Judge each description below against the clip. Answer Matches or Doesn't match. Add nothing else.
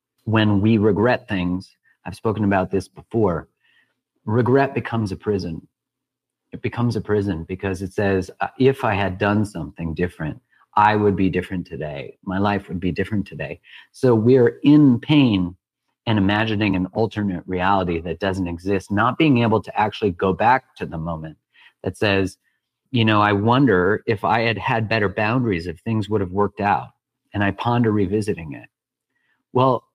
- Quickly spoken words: Doesn't match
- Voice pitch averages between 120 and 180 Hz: Doesn't match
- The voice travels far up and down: Doesn't match